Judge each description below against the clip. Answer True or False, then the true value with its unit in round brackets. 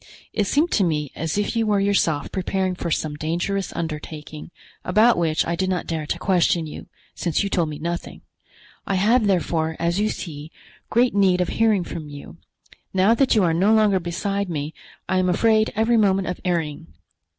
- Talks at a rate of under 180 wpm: False (190 wpm)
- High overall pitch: False (180 Hz)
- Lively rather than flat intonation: False (3.9 semitones)